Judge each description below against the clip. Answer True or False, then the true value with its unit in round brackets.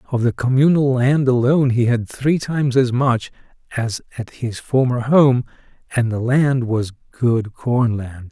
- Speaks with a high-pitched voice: False (125 Hz)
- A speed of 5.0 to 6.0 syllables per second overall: False (4.3 syllables/s)